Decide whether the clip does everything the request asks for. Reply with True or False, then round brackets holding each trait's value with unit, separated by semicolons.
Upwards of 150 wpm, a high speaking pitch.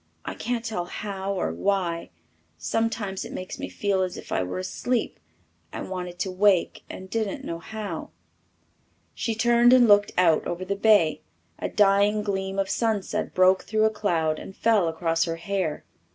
True (170 wpm; 195 Hz)